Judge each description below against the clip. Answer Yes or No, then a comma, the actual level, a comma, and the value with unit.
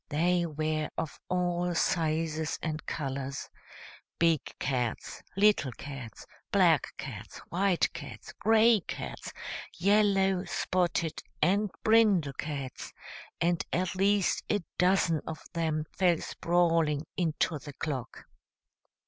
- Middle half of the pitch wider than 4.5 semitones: No, average, 3.3 semitones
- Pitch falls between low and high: Yes, medium, 170 Hz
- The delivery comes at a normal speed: No, slow, 105 wpm